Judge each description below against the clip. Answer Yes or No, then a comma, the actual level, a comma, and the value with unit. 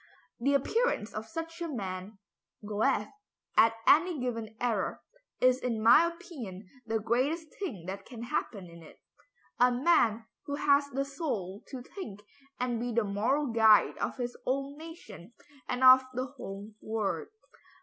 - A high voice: Yes, high, 245 Hz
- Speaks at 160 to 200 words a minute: No, average, 150 wpm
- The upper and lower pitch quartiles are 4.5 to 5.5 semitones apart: Yes, average, 4.8 semitones